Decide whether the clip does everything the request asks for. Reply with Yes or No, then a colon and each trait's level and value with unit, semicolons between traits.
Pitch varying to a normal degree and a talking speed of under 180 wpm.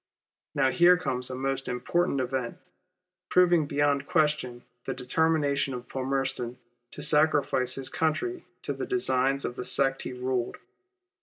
Yes: average, 3.2 semitones; average, 140 wpm